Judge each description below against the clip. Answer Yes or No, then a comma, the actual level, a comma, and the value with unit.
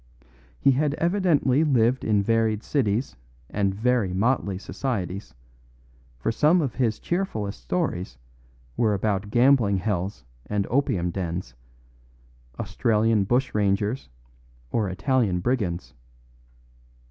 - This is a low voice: Yes, low, 110 Hz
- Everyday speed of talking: No, slow, 100 wpm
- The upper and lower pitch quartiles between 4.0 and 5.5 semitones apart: Yes, average, 4.9 semitones